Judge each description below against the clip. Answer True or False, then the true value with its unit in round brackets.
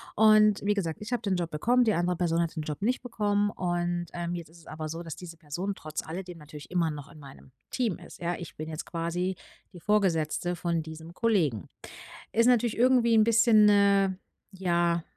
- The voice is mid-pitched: True (175 Hz)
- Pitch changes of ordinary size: True (4.2 semitones)